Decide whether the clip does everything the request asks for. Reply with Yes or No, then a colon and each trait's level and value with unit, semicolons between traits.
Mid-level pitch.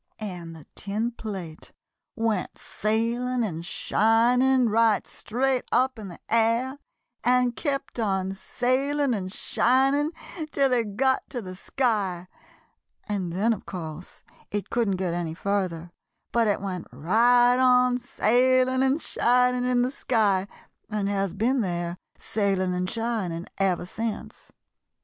No: high, 225 Hz